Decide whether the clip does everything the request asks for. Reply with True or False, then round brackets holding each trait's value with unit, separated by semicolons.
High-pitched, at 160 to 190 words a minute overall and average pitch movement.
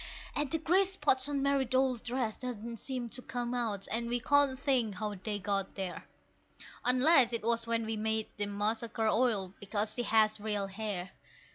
True (230 Hz; 180 wpm; 3.5 semitones)